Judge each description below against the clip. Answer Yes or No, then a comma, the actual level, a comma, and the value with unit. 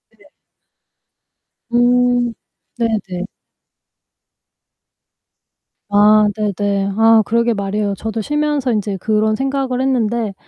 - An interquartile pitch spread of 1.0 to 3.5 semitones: Yes, average, 2.9 semitones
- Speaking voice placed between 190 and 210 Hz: No, high, 220 Hz